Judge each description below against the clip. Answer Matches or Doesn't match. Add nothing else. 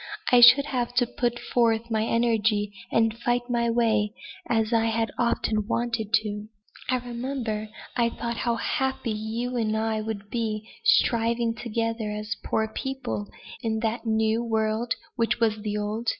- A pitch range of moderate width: Doesn't match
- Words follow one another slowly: Doesn't match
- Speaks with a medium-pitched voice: Doesn't match